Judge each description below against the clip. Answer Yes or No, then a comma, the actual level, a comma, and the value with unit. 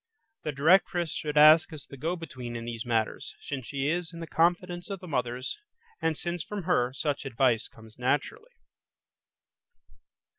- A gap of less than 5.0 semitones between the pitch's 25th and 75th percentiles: No, wide, 5.5 semitones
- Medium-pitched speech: Yes, medium, 150 Hz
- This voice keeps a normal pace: Yes, average, 160 wpm